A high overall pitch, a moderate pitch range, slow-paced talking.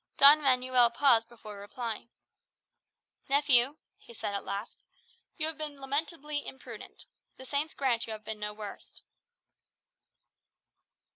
Yes: very high, 255 Hz; average, 4.4 semitones; slow, 125 wpm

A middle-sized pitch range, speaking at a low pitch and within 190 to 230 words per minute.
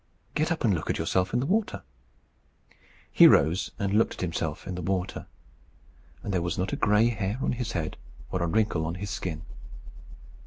Yes: average, 4.3 semitones; very low, 95 Hz; average, 195 wpm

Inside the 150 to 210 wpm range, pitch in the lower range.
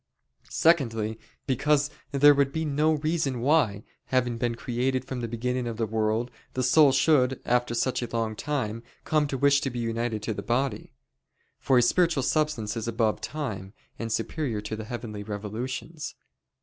Yes: average, 170 wpm; low, 125 Hz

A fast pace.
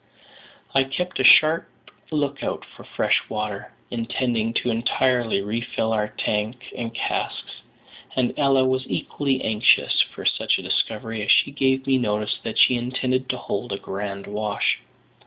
No: average, 155 wpm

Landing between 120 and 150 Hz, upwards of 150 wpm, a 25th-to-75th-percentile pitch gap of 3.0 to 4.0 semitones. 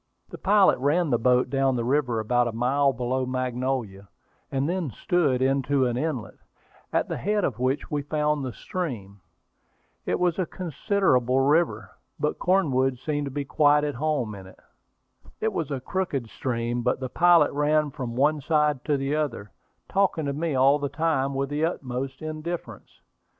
Yes: medium, 140 Hz; average, 175 wpm; average, 3.4 semitones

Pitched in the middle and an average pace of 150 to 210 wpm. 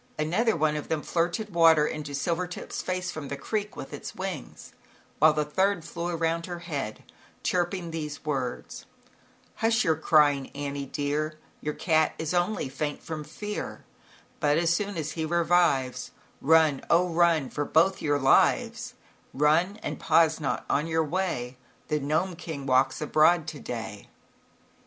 Yes: medium, 160 Hz; average, 155 wpm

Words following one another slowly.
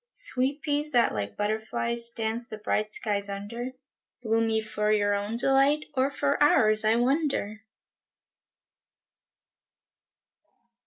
Yes: slow, 115 wpm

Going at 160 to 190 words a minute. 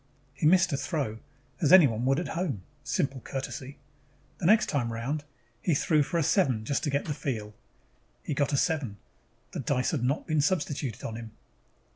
Yes: average, 185 wpm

